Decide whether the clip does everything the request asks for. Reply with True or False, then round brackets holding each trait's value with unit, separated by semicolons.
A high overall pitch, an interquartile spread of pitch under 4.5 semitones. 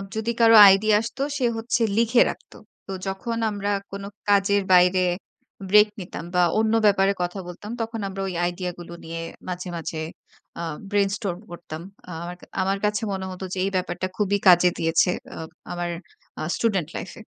True (195 Hz; 2.9 semitones)